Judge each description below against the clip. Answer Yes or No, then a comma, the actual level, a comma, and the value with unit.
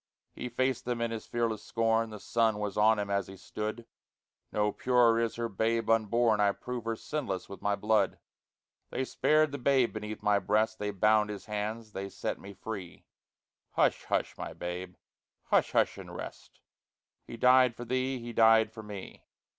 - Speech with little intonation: Yes, narrow, 2.1 semitones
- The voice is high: No, low, 110 Hz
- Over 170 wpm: Yes, average, 180 wpm